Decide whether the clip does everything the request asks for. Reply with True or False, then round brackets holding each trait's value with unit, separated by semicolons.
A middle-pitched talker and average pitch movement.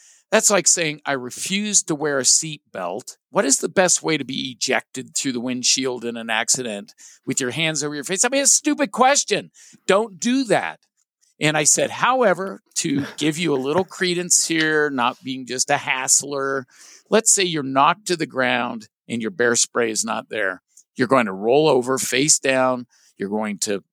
False (145 Hz; 6.0 semitones)